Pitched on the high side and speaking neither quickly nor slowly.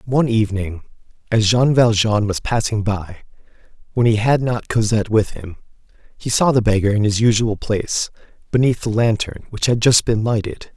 No: low, 110 Hz; average, 175 wpm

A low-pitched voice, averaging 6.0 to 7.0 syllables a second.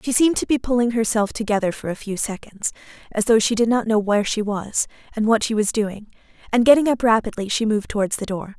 No: high, 220 Hz; 6.3 syllables/s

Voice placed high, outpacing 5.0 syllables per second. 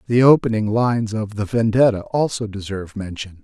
No: low, 110 Hz; 5.5 syllables/s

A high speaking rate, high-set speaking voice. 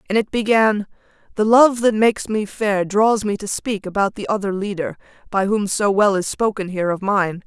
Yes: fast, 210 wpm; high, 205 Hz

